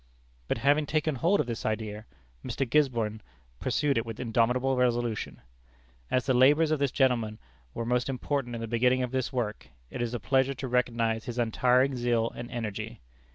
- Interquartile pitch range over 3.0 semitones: No, narrow, 2.5 semitones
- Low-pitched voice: Yes, low, 125 Hz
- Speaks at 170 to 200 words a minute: Yes, average, 180 wpm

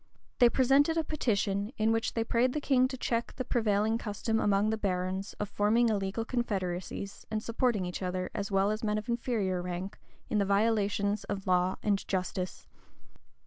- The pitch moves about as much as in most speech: Yes, average, 3.1 semitones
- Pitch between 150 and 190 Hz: No, high, 210 Hz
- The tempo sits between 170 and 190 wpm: Yes, average, 180 wpm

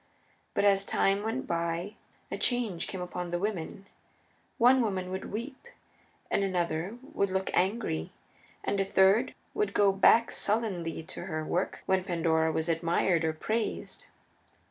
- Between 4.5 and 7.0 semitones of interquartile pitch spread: No, average, 3.8 semitones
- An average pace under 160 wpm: Yes, average, 145 wpm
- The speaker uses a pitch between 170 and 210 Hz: Yes, high, 190 Hz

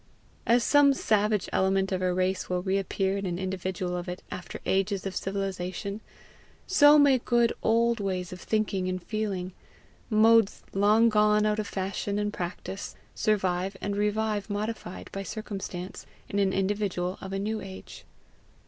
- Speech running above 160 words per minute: No, average, 155 wpm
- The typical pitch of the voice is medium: No, high, 195 Hz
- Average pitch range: No, narrow, 2.3 semitones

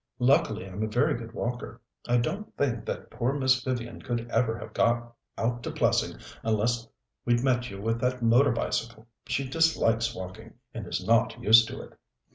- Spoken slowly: No, average, 180 wpm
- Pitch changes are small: Yes, narrow, 1.8 semitones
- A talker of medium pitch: No, low, 120 Hz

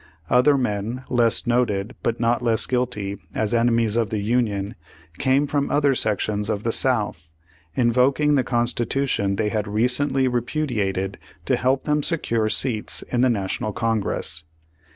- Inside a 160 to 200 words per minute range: No, average, 150 wpm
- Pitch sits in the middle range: No, low, 120 Hz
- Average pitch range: Yes, average, 3.3 semitones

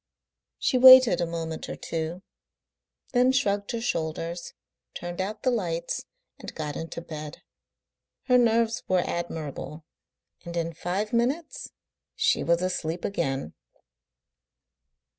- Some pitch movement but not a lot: No, wide, 6.0 semitones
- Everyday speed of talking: No, slow, 120 wpm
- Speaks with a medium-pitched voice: Yes, medium, 175 Hz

